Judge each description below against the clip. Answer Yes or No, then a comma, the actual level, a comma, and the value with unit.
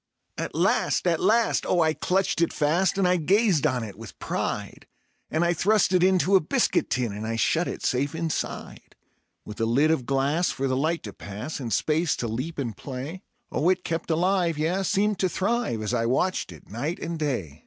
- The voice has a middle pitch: Yes, medium, 155 Hz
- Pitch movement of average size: No, wide, 6.5 semitones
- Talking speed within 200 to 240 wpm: Yes, fast, 205 wpm